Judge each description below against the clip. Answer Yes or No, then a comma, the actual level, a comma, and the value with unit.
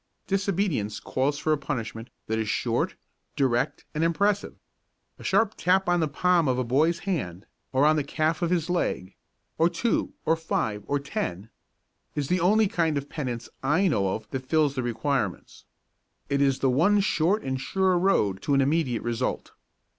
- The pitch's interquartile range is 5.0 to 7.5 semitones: Yes, wide, 5.6 semitones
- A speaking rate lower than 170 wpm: No, average, 175 wpm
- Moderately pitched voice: Yes, medium, 145 Hz